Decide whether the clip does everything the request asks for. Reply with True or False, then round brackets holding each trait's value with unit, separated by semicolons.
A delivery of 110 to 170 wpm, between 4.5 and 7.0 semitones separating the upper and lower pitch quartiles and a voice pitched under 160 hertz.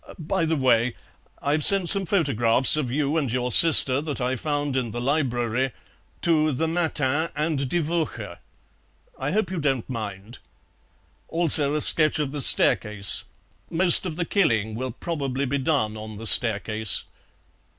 True (155 wpm; 4.8 semitones; 140 Hz)